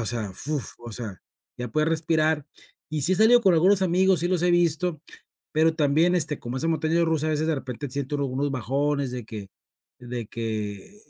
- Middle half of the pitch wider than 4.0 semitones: Yes, average, 5.0 semitones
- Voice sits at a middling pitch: Yes, medium, 150 Hz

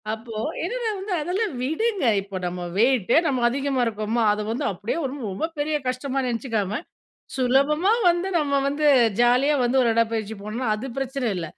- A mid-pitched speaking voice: No, very high, 255 Hz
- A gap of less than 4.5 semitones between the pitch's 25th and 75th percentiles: No, average, 4.8 semitones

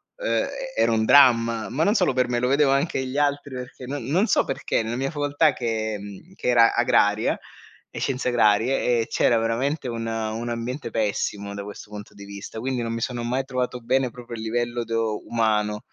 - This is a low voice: Yes, low, 120 Hz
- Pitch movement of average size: Yes, average, 3.0 semitones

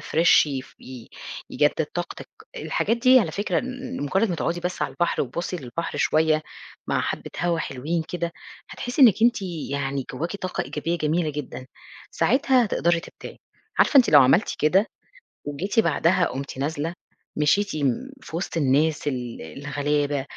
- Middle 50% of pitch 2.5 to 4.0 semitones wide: No, average, 5.0 semitones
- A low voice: No, medium, 165 Hz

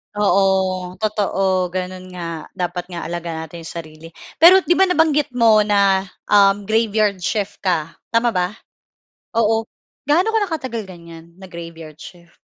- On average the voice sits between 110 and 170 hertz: No, high, 190 Hz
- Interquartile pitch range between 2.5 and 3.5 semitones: No, average, 4.4 semitones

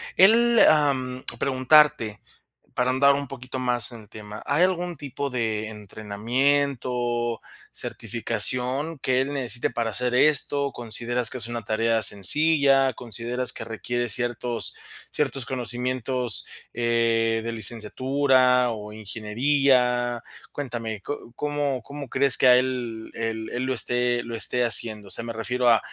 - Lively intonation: No, average, 2.8 semitones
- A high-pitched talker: No, low, 125 Hz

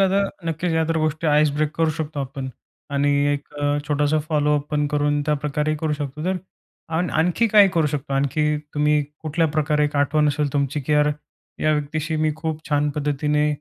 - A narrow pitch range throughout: Yes, narrow, 1.2 semitones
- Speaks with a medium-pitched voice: Yes, medium, 150 Hz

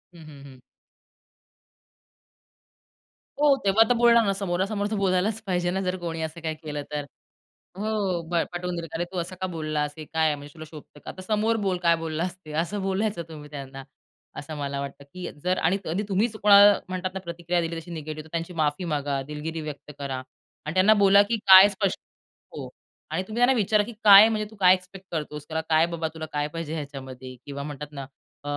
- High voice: No, medium, 170 Hz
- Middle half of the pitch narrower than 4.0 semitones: No, average, 4.3 semitones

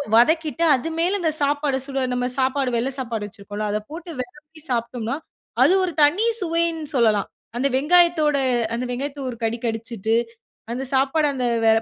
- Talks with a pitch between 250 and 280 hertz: Yes, very high, 270 Hz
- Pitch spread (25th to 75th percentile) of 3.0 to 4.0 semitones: No, average, 5.0 semitones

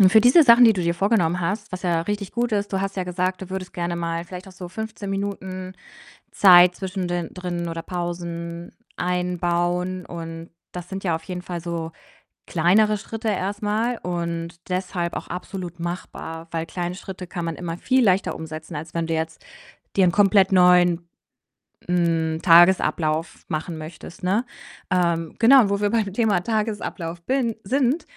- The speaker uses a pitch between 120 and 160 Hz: No, medium, 180 Hz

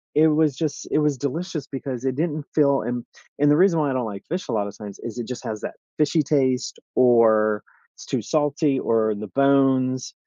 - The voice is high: No, low, 135 Hz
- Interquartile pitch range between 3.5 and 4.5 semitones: Yes, average, 4.1 semitones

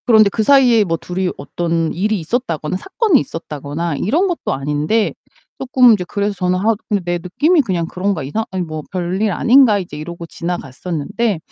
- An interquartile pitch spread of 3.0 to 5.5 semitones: Yes, average, 5.1 semitones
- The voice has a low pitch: No, medium, 185 Hz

